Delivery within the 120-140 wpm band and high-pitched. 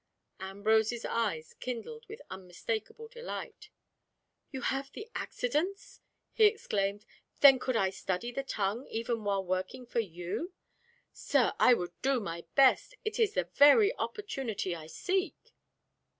Yes: slow, 135 wpm; high, 235 Hz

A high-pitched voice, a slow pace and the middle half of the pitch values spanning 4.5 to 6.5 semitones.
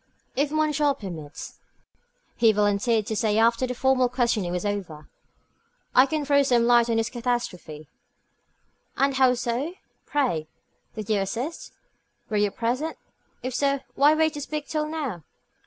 No: high, 240 Hz; average, 150 wpm; average, 5.1 semitones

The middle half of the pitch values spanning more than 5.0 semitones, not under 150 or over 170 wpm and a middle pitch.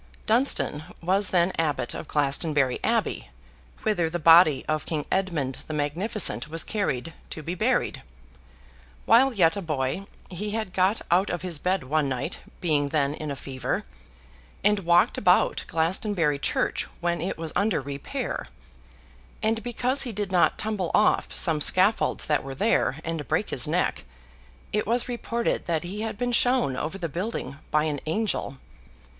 Yes: wide, 5.6 semitones; average, 160 wpm; medium, 170 Hz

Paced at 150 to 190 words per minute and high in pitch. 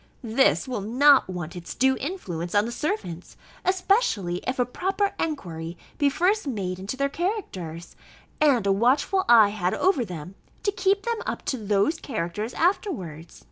Yes: average, 160 wpm; high, 245 Hz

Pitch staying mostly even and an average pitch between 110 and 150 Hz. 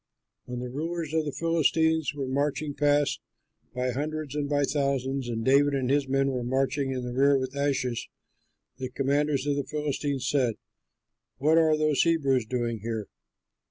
Yes: narrow, 2.3 semitones; medium, 140 Hz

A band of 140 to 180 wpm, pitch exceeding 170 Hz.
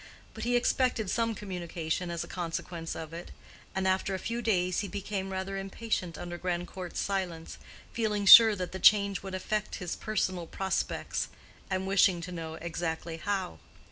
Yes: average, 165 wpm; high, 190 Hz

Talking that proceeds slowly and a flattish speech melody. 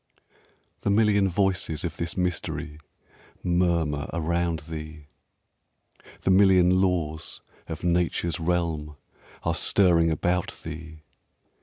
Yes: slow, 100 wpm; narrow, 2.2 semitones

